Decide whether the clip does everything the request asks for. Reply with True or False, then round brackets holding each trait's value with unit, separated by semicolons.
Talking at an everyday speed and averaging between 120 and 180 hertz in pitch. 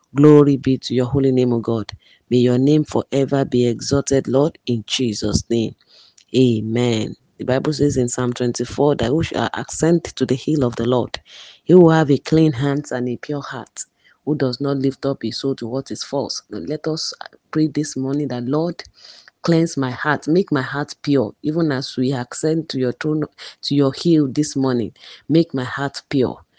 True (195 wpm; 135 Hz)